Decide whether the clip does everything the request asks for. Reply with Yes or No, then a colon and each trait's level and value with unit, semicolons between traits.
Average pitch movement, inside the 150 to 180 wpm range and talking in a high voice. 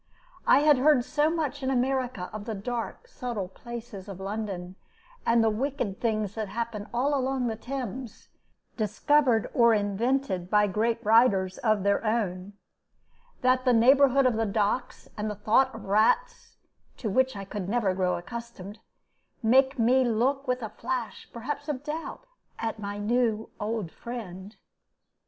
Yes: average, 3.7 semitones; average, 155 wpm; high, 230 Hz